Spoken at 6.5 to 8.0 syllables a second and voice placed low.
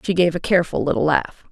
No: 6.8 syllables/s; medium, 165 Hz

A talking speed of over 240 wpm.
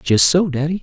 No: fast, 220 wpm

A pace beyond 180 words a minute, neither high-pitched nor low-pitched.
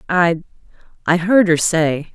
No: slow, 110 wpm; medium, 170 Hz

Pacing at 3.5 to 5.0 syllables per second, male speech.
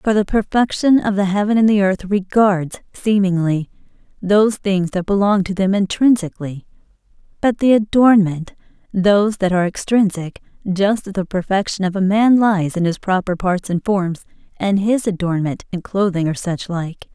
No: 4.9 syllables/s; female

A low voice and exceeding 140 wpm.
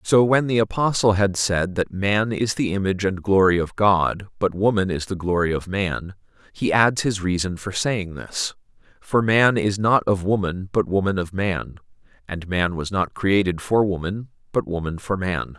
Yes: low, 100 Hz; average, 190 wpm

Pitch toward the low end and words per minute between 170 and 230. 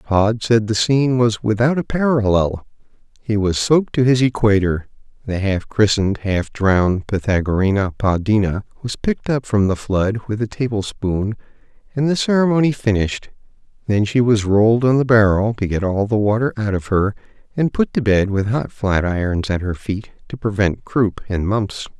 Yes: low, 110 Hz; average, 175 wpm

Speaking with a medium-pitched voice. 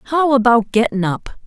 No: high, 240 Hz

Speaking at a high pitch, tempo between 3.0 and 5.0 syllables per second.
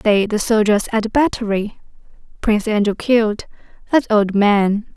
Yes: high, 215 Hz; 4.8 syllables/s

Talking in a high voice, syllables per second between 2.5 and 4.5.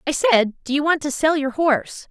No: very high, 290 Hz; 5.4 syllables/s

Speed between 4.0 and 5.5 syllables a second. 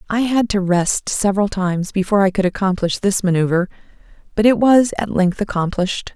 No: 5.8 syllables/s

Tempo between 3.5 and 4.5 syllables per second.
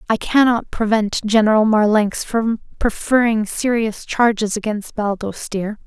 Yes: 4.2 syllables/s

